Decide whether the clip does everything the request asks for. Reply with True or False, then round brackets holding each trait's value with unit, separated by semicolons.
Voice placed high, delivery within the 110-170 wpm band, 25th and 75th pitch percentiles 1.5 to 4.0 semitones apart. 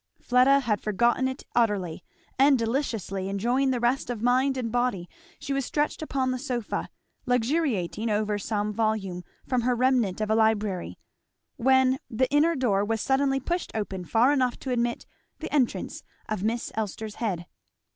True (240 Hz; 160 wpm; 3.7 semitones)